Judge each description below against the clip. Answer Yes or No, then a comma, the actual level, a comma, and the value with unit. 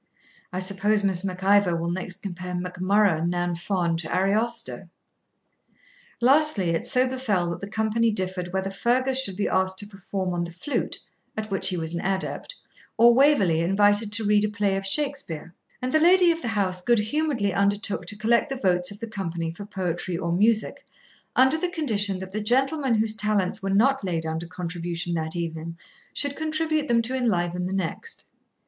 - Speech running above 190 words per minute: No, average, 185 wpm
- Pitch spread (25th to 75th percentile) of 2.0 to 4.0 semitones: No, average, 4.6 semitones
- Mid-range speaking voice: No, high, 200 Hz